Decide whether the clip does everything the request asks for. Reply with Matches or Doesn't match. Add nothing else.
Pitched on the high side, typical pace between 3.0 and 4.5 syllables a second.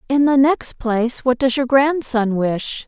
Matches